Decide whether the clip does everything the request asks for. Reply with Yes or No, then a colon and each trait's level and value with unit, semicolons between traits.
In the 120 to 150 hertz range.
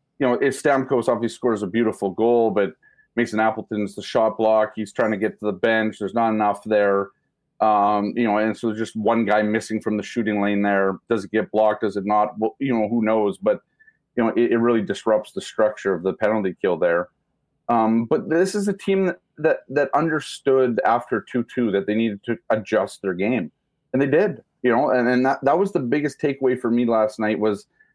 No: low, 110 Hz